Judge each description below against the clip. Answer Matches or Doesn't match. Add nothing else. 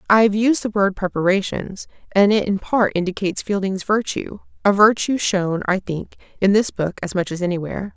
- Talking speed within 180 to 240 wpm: Matches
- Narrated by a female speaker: Matches